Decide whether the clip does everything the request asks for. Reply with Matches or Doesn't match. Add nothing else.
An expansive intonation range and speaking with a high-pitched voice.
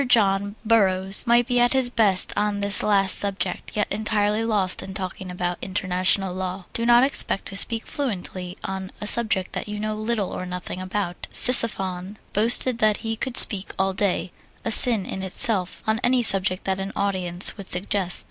Doesn't match